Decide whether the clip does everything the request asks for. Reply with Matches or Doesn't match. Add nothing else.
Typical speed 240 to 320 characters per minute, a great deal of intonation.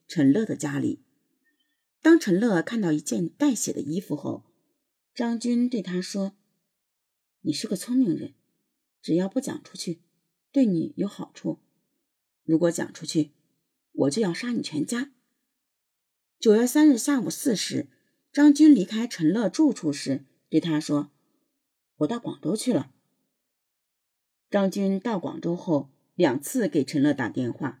Doesn't match